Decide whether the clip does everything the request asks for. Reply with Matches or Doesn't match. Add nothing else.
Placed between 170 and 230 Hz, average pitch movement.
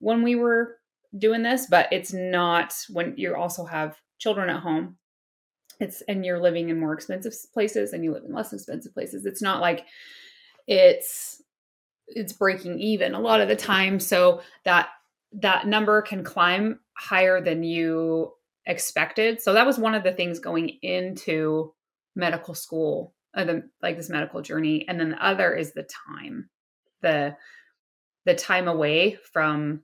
Matches